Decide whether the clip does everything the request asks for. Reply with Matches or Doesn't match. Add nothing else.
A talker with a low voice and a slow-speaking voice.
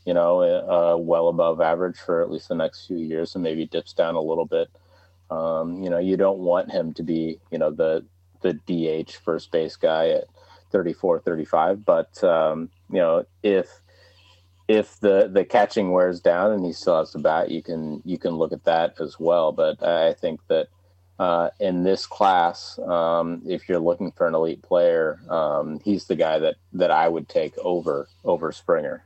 Doesn't match